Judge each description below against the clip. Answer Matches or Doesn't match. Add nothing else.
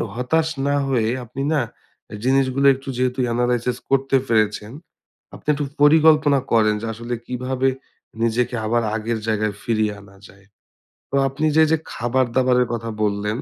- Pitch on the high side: Doesn't match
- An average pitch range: Matches